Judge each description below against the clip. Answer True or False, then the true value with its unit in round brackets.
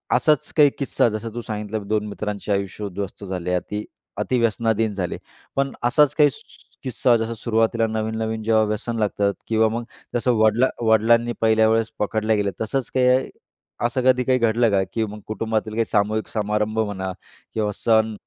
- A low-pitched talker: True (110 Hz)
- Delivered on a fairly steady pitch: True (1.8 semitones)